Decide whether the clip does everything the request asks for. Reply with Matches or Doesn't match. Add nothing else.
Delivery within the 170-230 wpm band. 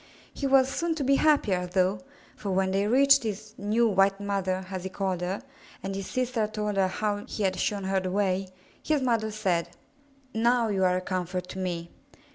Matches